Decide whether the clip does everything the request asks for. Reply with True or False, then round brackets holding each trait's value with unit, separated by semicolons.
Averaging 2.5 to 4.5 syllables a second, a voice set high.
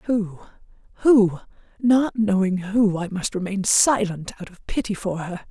True (4.3 syllables/s; 200 Hz)